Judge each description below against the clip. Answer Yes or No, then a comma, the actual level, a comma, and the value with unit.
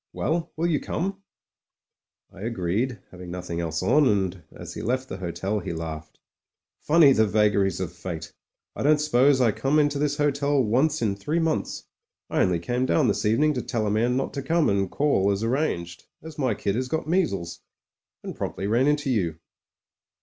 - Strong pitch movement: Yes, wide, 7.4 semitones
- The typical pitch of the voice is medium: No, low, 120 Hz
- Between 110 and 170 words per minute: No, average, 195 wpm